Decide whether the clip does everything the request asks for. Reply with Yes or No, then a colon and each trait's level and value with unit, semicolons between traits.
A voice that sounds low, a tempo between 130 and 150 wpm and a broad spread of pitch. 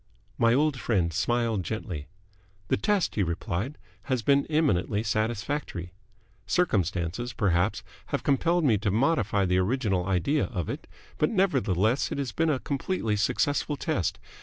Yes: low, 115 Hz; average, 140 wpm; wide, 7.0 semitones